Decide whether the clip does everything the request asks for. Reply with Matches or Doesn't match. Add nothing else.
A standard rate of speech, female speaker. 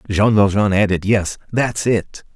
Doesn't match